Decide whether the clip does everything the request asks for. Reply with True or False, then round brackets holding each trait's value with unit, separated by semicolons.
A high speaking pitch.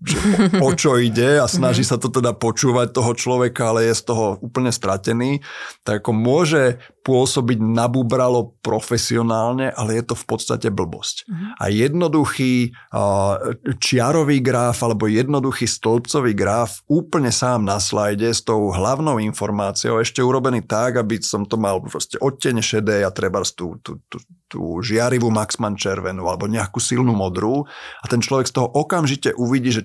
False (120 Hz)